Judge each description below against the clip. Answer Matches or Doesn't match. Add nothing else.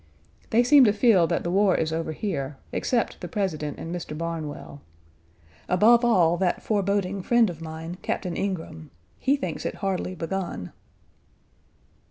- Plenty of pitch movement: Doesn't match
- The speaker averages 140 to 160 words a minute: Matches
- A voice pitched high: Doesn't match